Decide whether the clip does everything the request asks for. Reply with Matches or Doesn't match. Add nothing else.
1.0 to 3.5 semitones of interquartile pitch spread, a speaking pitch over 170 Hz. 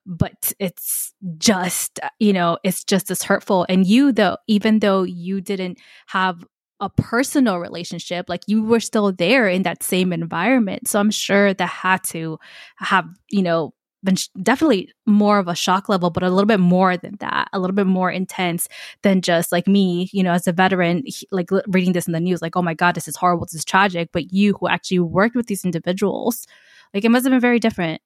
Matches